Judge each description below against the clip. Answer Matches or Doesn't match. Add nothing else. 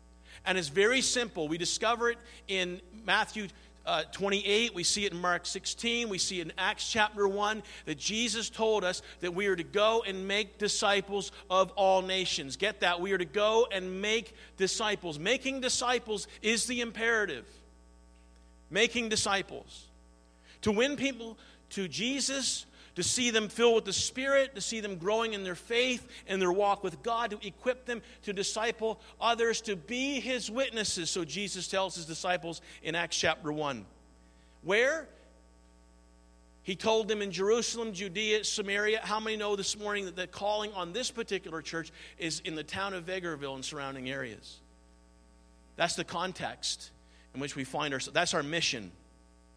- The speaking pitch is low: Doesn't match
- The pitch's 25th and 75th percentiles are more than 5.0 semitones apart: Matches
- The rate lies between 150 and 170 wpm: Matches